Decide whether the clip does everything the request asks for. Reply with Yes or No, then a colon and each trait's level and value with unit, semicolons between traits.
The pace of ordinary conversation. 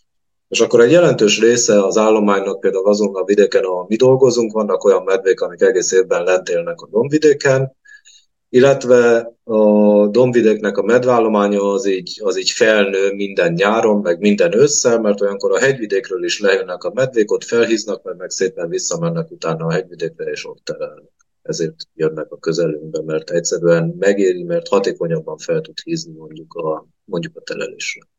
No: fast, 160 wpm